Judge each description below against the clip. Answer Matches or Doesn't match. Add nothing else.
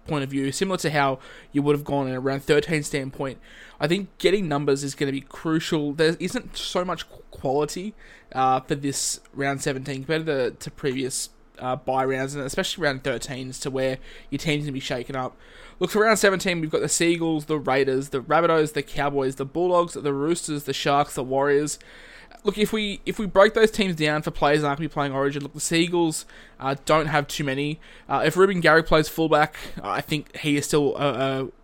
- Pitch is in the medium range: Matches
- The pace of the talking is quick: Matches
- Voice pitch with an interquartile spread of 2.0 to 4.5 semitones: Matches